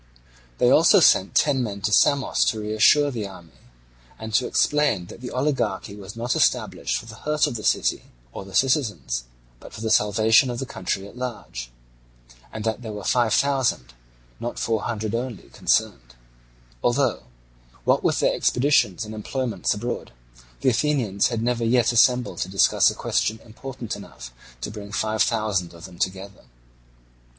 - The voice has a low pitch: Yes, low, 110 Hz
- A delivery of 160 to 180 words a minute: Yes, average, 165 wpm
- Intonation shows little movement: No, average, 3.8 semitones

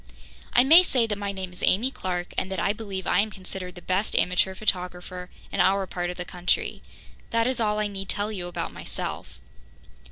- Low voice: No, high, 190 Hz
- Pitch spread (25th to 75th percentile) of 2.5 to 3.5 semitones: Yes, average, 2.8 semitones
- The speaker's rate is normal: No, fast, 210 wpm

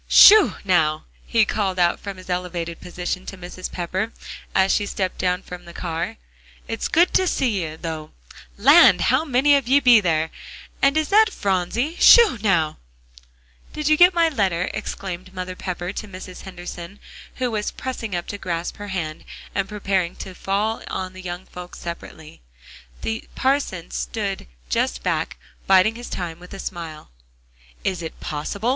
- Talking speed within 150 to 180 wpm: Yes, average, 165 wpm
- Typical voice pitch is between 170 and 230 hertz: Yes, medium, 185 Hz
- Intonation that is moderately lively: Yes, average, 4.3 semitones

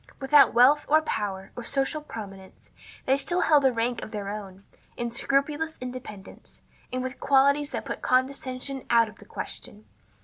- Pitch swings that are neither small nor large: Yes, average, 4.4 semitones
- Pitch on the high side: Yes, very high, 255 Hz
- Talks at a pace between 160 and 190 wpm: Yes, average, 165 wpm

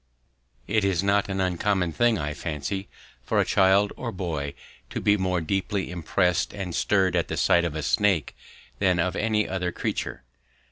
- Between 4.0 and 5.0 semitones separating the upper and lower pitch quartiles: No, narrow, 2.6 semitones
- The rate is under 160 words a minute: No, average, 175 wpm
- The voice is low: Yes, very low, 95 Hz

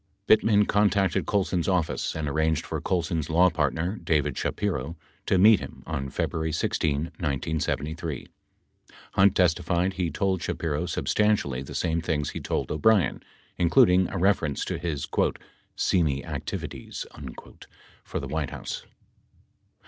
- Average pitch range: Yes, average, 3.7 semitones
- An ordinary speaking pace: No, slow, 130 wpm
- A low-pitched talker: Yes, very low, 85 Hz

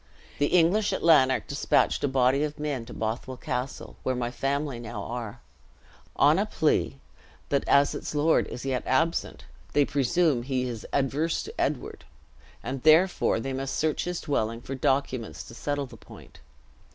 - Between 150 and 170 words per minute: Yes, average, 165 wpm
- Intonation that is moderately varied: Yes, average, 3.2 semitones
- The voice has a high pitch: No, low, 135 Hz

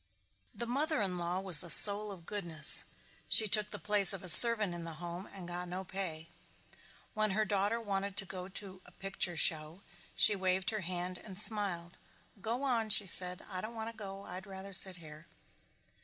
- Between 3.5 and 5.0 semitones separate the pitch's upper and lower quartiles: No, average, 3.0 semitones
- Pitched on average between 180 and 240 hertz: Yes, high, 190 Hz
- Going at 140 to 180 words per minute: No, average, 195 wpm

